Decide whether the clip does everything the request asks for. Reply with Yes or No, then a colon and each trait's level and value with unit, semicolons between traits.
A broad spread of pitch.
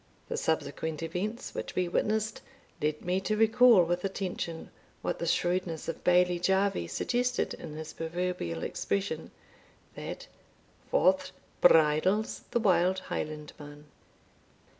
No: average, 3.2 semitones